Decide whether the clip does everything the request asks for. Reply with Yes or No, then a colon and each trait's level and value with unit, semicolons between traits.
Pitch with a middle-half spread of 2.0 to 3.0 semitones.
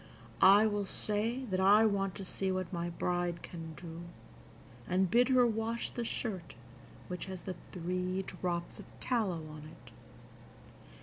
No: average, 3.5 semitones